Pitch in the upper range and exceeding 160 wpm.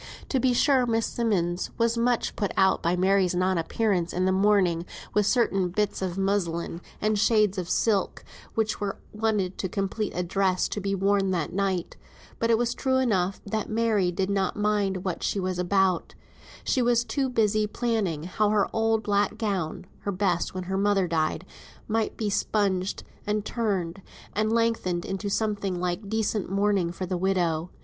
Yes: high, 200 Hz; average, 175 wpm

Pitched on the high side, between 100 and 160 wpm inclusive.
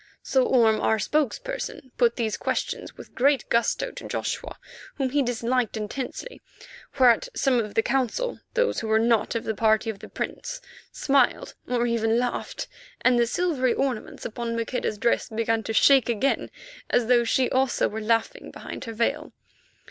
No: high, 240 Hz; average, 170 wpm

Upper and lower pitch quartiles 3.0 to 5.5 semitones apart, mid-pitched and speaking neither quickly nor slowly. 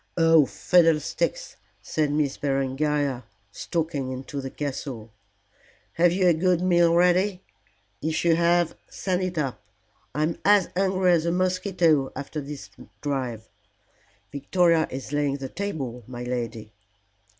No: average, 4.5 semitones; medium, 155 Hz; slow, 130 wpm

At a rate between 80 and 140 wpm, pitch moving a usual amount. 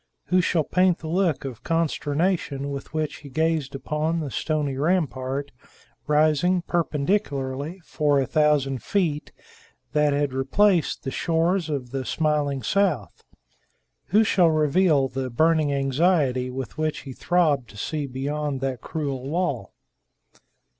Yes: slow, 135 wpm; average, 3.4 semitones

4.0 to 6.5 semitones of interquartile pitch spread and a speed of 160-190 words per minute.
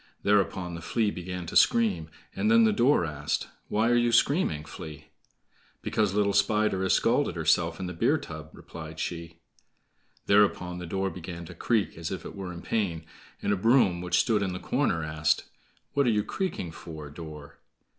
Yes: average, 4.4 semitones; average, 185 wpm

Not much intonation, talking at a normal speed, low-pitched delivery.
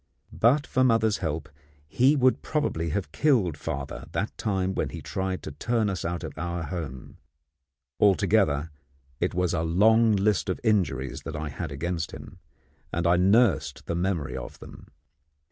No: average, 5.1 semitones; average, 160 wpm; very low, 90 Hz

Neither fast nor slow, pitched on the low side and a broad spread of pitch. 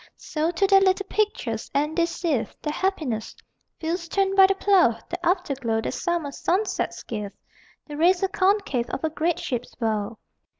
No: average, 165 wpm; very high, 335 Hz; wide, 6.7 semitones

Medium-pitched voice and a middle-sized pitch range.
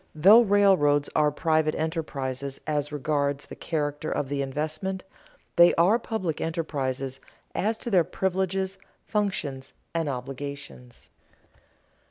Yes: medium, 155 Hz; average, 4.9 semitones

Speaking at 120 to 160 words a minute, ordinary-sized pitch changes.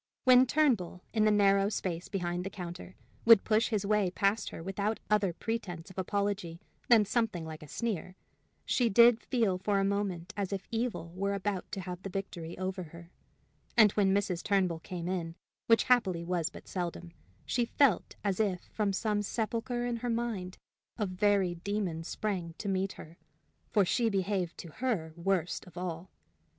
No: average, 175 wpm; average, 3.3 semitones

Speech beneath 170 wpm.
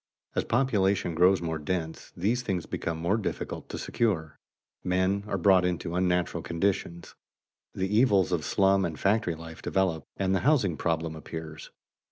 Yes: average, 155 wpm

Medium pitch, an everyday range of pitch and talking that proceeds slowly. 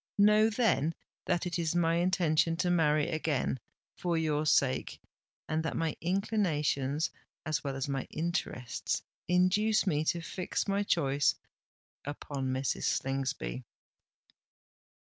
Yes: medium, 160 Hz; average, 3.8 semitones; slow, 115 wpm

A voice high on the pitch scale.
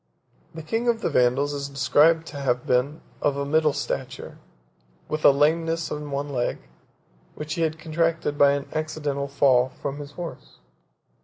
No: medium, 145 Hz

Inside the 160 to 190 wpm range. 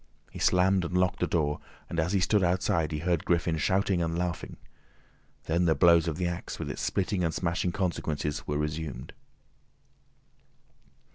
Yes: average, 165 wpm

